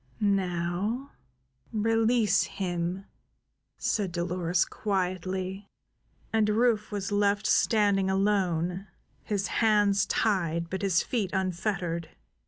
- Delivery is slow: Yes, slow, 90 wpm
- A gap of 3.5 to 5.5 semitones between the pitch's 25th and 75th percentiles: No, narrow, 2.6 semitones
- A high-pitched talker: Yes, high, 195 Hz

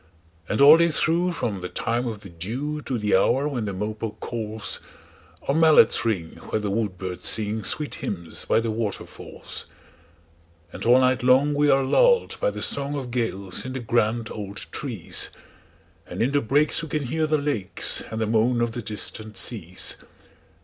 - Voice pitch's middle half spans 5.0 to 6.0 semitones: Yes, wide, 5.5 semitones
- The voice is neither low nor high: No, low, 115 Hz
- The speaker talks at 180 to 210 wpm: No, average, 160 wpm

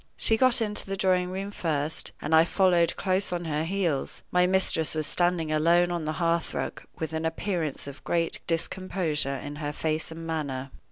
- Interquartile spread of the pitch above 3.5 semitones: No, average, 2.9 semitones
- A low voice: No, medium, 165 Hz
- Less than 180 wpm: No, average, 185 wpm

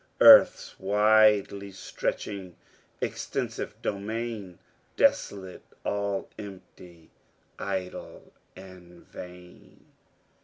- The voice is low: Yes, very low, 95 Hz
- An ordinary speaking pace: No, slow, 65 wpm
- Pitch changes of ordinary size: No, narrow, 2.0 semitones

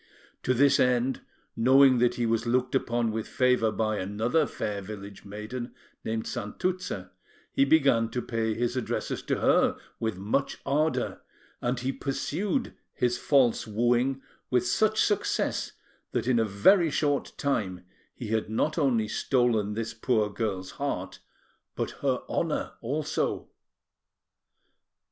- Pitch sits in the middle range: No, low, 120 Hz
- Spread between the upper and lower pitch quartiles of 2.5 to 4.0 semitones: Yes, average, 3.6 semitones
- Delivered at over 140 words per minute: No, slow, 135 wpm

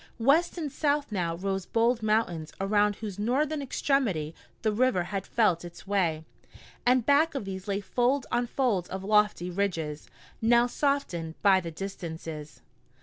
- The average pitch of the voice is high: Yes, high, 205 Hz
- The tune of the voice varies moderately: No, wide, 5.7 semitones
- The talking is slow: No, average, 150 wpm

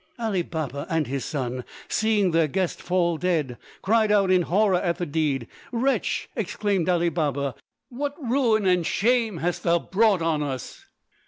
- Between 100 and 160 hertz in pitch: No, medium, 175 Hz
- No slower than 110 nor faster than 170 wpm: Yes, average, 160 wpm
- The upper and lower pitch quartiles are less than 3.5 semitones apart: No, average, 5.2 semitones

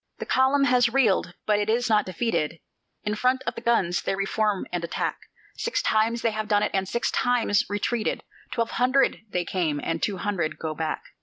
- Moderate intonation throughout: Yes, average, 4.3 semitones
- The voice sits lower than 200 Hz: No, high, 210 Hz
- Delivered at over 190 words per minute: Yes, fast, 205 wpm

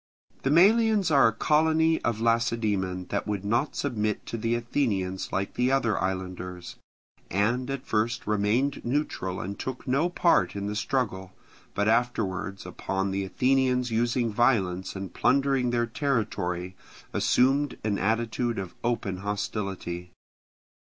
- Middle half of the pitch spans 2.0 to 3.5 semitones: No, average, 4.9 semitones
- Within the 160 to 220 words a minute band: No, slow, 135 wpm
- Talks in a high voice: No, low, 115 Hz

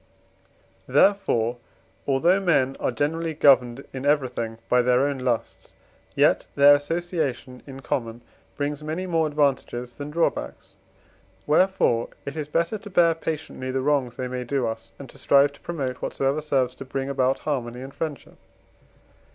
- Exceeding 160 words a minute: No, average, 155 wpm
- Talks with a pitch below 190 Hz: Yes, medium, 140 Hz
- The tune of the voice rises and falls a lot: No, average, 3.3 semitones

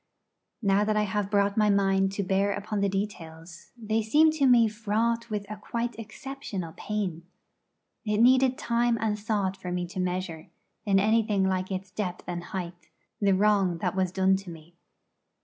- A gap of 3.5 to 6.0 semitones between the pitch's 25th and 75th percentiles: No, average, 2.7 semitones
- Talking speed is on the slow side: No, average, 175 wpm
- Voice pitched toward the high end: Yes, high, 200 Hz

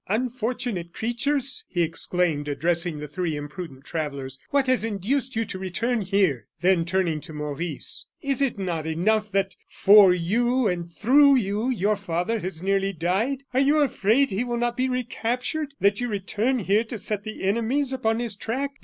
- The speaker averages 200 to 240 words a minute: No, average, 170 wpm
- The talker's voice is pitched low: No, high, 205 Hz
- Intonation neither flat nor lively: No, wide, 5.9 semitones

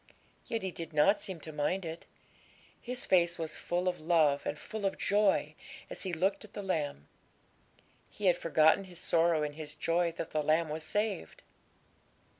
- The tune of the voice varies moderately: Yes, average, 3.5 semitones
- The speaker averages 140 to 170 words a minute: No, average, 180 wpm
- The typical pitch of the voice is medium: Yes, medium, 170 Hz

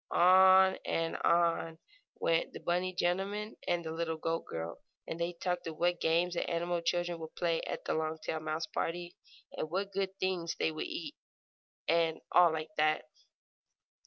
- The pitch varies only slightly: Yes, narrow, 1.7 semitones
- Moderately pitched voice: Yes, medium, 170 Hz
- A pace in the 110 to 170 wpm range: Yes, average, 165 wpm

